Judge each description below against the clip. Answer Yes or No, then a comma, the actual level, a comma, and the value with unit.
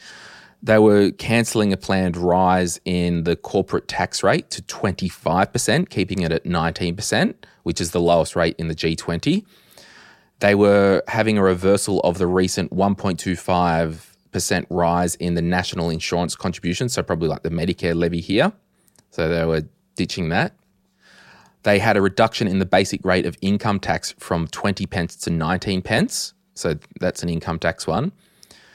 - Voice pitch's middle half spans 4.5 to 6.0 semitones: No, average, 2.7 semitones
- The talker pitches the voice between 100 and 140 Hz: No, very low, 90 Hz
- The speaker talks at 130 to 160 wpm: Yes, average, 155 wpm